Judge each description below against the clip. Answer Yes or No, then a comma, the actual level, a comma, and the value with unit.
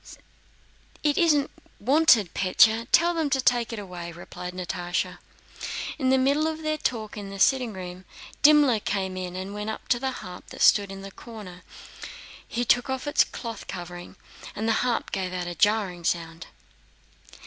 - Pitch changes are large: Yes, wide, 6.2 semitones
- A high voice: Yes, high, 215 Hz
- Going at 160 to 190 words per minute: Yes, average, 175 wpm